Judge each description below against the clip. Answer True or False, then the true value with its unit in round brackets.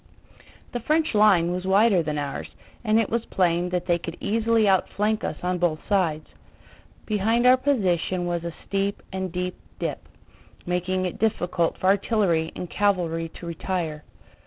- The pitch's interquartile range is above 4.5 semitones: False (3.6 semitones)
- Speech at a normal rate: True (160 wpm)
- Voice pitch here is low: False (185 Hz)